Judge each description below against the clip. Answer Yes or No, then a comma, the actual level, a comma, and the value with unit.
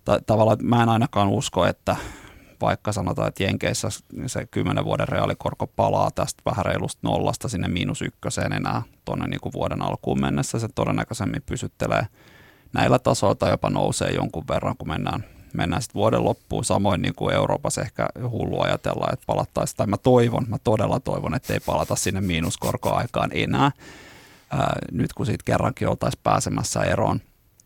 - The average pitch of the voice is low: Yes, low, 115 Hz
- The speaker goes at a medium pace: No, fast, 160 wpm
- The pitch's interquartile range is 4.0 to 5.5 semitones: Yes, average, 4.5 semitones